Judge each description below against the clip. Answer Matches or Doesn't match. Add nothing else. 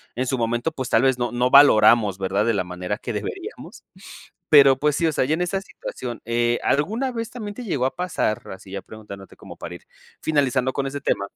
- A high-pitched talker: Doesn't match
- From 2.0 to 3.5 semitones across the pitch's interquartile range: Doesn't match